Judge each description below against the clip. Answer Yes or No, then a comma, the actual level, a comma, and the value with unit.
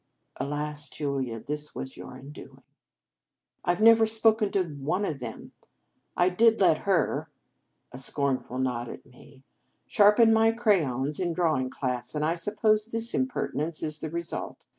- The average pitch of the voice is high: No, medium, 155 Hz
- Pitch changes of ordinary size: No, wide, 7.3 semitones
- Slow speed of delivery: No, average, 160 wpm